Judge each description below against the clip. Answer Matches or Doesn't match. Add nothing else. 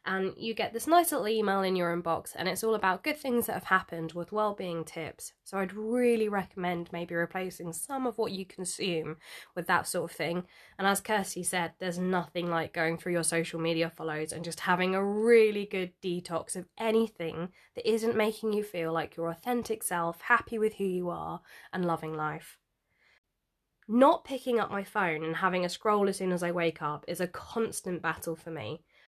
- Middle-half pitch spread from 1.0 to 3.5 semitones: Doesn't match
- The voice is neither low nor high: Matches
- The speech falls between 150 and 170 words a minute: Doesn't match